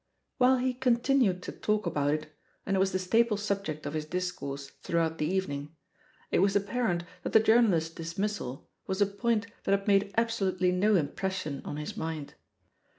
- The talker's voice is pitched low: No, high, 190 Hz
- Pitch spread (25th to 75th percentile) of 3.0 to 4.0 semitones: No, average, 4.7 semitones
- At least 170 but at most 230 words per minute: Yes, average, 175 wpm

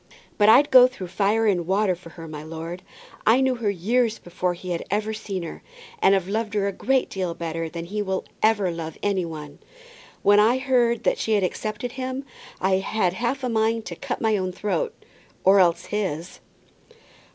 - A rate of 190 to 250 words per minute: Yes, average, 195 wpm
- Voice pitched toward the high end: Yes, high, 200 Hz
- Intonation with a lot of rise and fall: No, average, 4.1 semitones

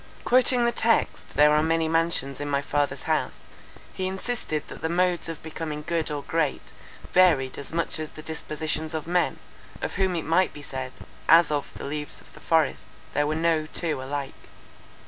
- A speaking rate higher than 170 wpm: Yes, average, 185 wpm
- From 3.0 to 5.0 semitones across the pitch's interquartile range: No, narrow, 2.5 semitones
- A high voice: No, medium, 160 Hz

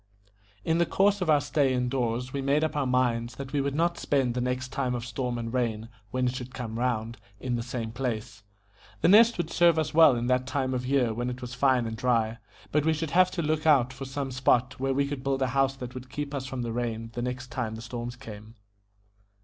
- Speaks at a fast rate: Yes, fast, 245 wpm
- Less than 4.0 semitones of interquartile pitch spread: Yes, average, 2.7 semitones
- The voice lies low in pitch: Yes, low, 130 Hz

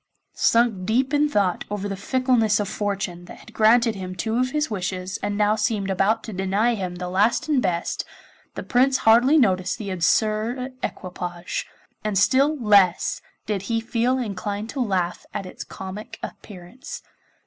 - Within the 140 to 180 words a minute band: Yes, average, 165 wpm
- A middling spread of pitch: Yes, average, 4.1 semitones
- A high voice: Yes, high, 210 Hz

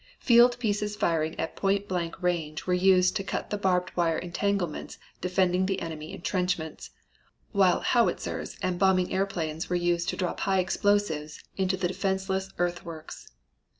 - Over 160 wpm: No, average, 150 wpm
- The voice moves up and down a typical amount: No, narrow, 2.2 semitones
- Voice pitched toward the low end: No, medium, 185 Hz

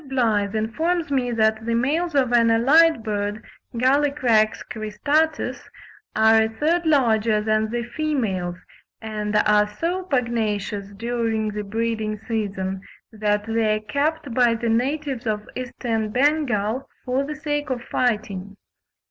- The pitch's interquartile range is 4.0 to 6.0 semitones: Yes, average, 4.3 semitones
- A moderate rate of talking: No, slow, 130 wpm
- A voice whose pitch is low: No, high, 230 Hz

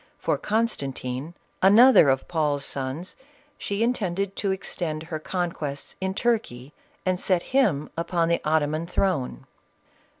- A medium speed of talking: No, slow, 125 wpm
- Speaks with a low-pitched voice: No, medium, 170 Hz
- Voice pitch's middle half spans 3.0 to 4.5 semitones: No, average, 5.1 semitones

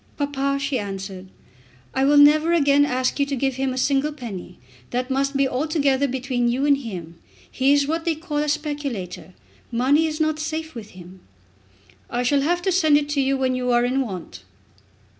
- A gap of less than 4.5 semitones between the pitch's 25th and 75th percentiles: Yes, average, 3.0 semitones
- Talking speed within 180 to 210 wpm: Yes, average, 190 wpm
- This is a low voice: No, very high, 275 Hz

